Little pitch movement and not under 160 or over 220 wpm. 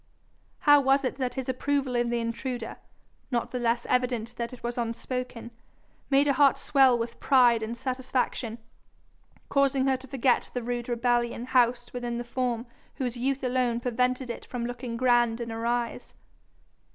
Yes: narrow, 1.6 semitones; average, 165 wpm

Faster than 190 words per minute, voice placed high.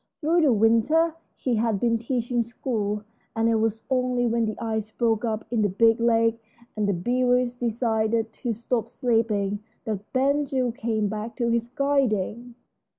No: average, 165 wpm; high, 230 Hz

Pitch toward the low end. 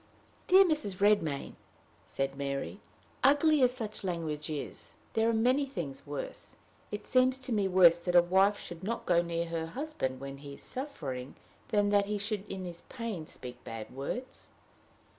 No: high, 190 Hz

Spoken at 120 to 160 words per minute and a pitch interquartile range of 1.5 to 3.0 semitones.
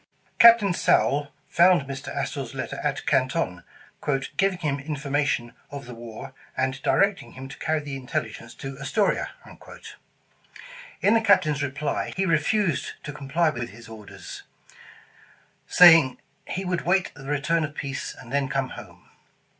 No: average, 145 wpm; average, 4.2 semitones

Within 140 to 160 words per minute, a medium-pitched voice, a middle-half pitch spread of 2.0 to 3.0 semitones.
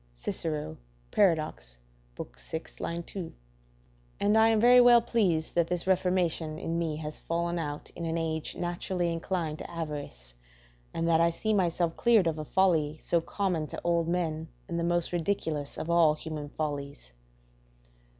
Yes: average, 155 wpm; medium, 170 Hz; narrow, 2.5 semitones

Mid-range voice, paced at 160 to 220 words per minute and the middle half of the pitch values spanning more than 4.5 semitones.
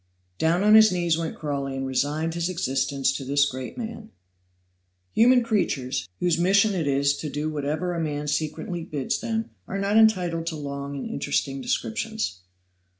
Yes: medium, 160 Hz; average, 165 wpm; average, 4.9 semitones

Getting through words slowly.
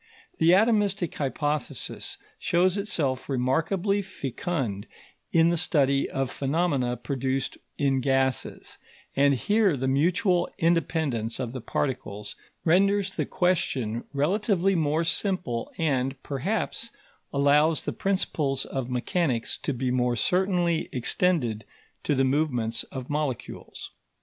Yes: slow, 115 wpm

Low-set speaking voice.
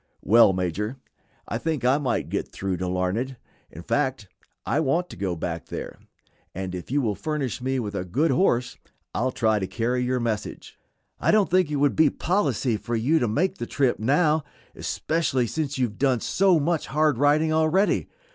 Yes: low, 130 Hz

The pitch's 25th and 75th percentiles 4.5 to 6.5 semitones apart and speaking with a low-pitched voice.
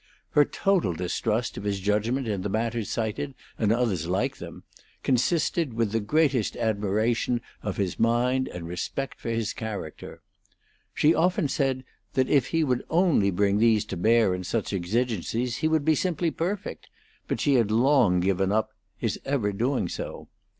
Yes: average, 4.9 semitones; low, 115 Hz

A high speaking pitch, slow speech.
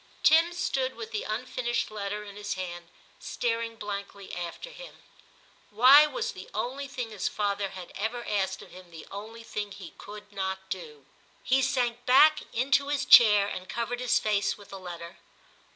No: high, 215 Hz; average, 170 wpm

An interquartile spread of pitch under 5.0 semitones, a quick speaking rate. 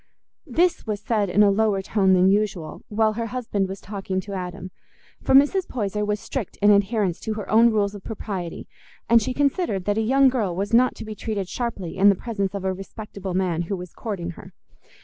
Yes: average, 2.7 semitones; fast, 210 wpm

